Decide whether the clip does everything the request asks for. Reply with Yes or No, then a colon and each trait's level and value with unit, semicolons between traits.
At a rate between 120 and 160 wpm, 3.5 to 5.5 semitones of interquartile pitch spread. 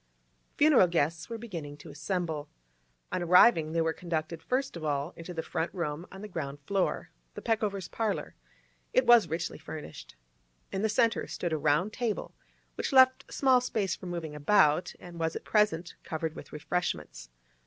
No: average, 170 wpm; average, 4.9 semitones